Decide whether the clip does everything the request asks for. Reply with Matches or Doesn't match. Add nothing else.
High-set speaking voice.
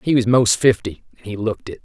Doesn't match